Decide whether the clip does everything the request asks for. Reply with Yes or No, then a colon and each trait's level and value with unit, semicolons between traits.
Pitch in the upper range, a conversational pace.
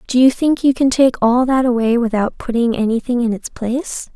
No: high, 245 Hz; fast, 215 wpm